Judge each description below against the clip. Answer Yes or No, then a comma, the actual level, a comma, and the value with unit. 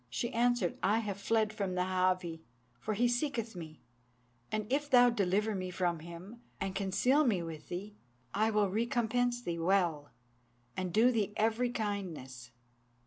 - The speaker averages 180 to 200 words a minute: No, average, 155 wpm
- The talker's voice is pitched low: No, high, 205 Hz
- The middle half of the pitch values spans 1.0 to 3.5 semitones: No, average, 4.5 semitones